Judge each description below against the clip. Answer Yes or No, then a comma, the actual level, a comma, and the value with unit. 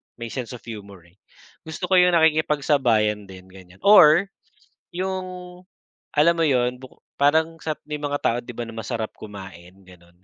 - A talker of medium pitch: No, low, 125 Hz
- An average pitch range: No, wide, 7.4 semitones